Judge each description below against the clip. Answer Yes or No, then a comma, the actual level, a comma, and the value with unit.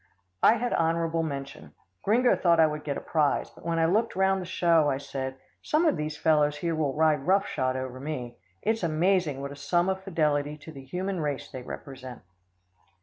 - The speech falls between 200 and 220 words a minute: Yes, fast, 205 wpm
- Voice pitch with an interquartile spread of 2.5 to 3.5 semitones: No, average, 4.2 semitones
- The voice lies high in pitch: No, medium, 155 Hz